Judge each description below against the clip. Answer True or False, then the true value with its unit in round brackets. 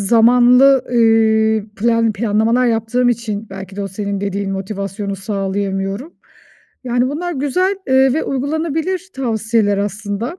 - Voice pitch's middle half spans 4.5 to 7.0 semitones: False (4.0 semitones)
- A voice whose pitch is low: False (225 Hz)